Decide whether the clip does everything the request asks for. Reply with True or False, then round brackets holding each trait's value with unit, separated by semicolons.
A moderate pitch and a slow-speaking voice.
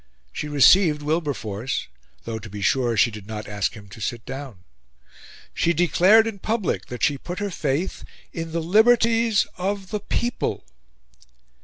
False (155 Hz; 155 wpm)